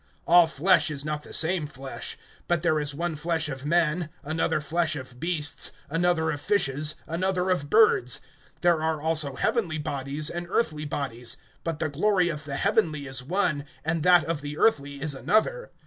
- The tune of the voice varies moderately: Yes, average, 3.1 semitones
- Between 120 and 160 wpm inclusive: No, average, 180 wpm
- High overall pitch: No, medium, 155 Hz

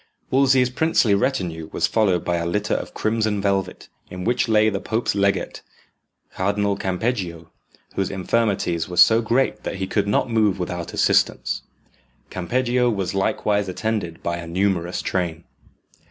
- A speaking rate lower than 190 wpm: Yes, average, 145 wpm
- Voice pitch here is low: Yes, low, 100 Hz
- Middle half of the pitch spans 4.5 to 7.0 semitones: No, average, 3.8 semitones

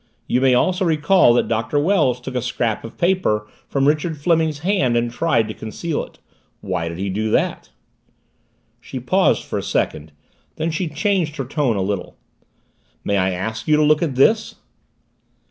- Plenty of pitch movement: Yes, wide, 6.4 semitones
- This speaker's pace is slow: No, average, 180 wpm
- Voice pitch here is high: No, low, 135 Hz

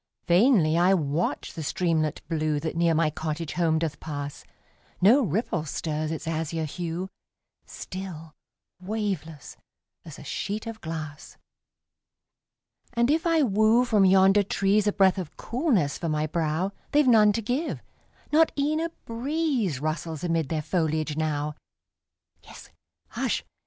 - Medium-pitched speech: Yes, medium, 170 Hz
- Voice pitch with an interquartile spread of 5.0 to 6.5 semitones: Yes, wide, 5.4 semitones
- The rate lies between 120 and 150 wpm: Yes, average, 140 wpm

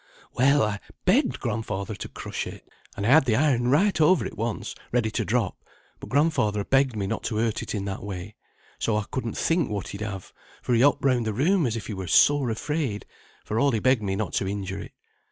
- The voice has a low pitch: Yes, low, 115 Hz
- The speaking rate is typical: No, fast, 225 wpm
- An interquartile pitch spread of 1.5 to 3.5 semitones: No, average, 4.8 semitones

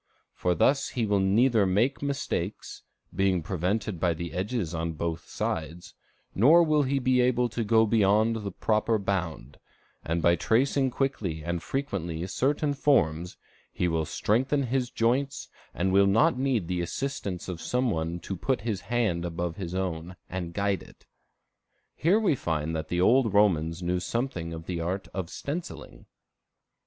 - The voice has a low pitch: Yes, low, 100 Hz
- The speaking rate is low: No, average, 160 wpm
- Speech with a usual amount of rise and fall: No, wide, 6.3 semitones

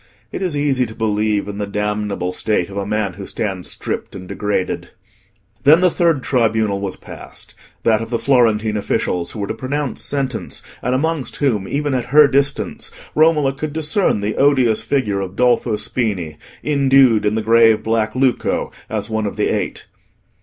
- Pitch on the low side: Yes, low, 115 Hz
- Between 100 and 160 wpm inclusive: No, average, 175 wpm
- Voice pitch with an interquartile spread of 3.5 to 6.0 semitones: Yes, average, 4.7 semitones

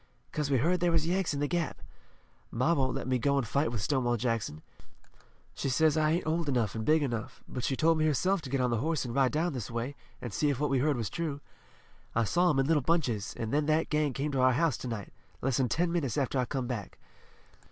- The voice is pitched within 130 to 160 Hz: Yes, medium, 140 Hz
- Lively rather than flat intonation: No, average, 4.2 semitones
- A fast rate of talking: Yes, fast, 255 wpm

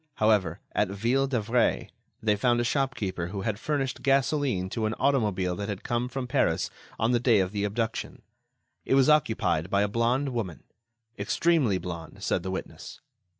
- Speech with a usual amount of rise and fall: Yes, average, 4.2 semitones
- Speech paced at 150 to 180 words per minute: Yes, average, 165 wpm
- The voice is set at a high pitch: No, low, 110 Hz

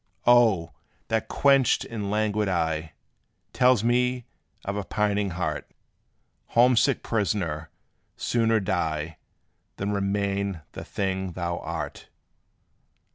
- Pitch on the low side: Yes, low, 100 Hz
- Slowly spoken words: Yes, slow, 100 wpm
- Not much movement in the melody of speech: No, average, 4.4 semitones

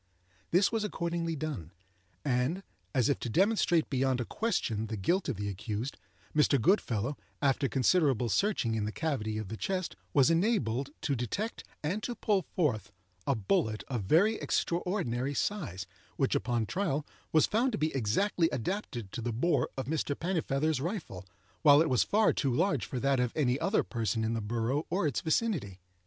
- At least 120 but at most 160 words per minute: No, average, 175 wpm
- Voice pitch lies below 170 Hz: Yes, medium, 140 Hz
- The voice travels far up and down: Yes, wide, 7.1 semitones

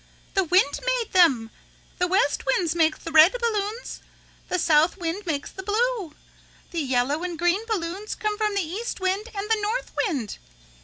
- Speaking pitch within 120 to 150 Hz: No, very high, 370 Hz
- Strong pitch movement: No, average, 4.5 semitones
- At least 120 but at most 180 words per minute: Yes, average, 170 wpm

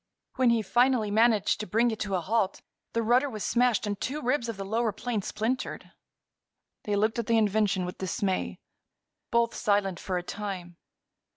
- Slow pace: No, average, 180 wpm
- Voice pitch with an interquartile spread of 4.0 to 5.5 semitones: No, average, 3.1 semitones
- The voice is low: No, high, 215 Hz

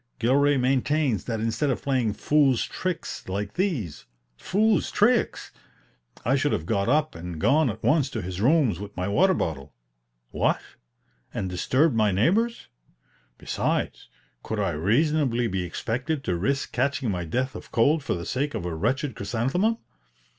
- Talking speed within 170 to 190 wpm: No, average, 155 wpm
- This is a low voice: Yes, low, 125 Hz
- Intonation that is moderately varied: No, wide, 6.7 semitones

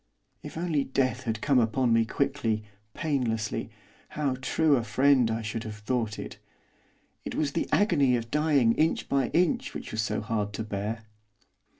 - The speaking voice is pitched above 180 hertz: No, low, 125 Hz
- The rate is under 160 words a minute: No, average, 170 wpm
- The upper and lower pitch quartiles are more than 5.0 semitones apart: No, average, 4.3 semitones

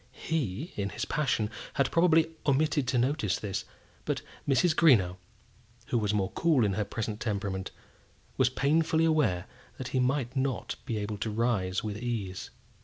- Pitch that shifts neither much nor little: No, wide, 5.9 semitones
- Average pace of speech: Yes, average, 160 wpm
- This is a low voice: Yes, low, 120 Hz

